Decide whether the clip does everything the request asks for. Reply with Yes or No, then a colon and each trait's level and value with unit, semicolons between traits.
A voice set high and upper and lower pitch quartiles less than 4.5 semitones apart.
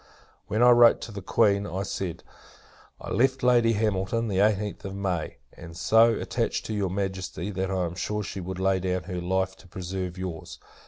No: very low, 95 Hz; narrow, 2.5 semitones